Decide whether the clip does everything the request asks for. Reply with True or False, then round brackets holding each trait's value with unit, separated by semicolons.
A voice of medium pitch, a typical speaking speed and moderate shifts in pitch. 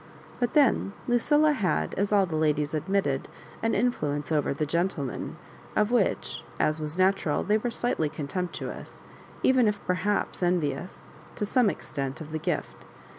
False (180 Hz; 150 wpm; 5.8 semitones)